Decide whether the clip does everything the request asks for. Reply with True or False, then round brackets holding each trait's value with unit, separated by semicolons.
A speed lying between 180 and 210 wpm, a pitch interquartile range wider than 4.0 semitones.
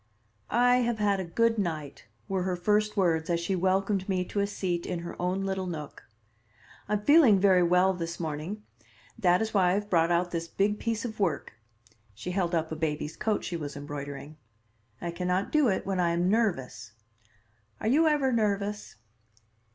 False (190 wpm; 3.5 semitones)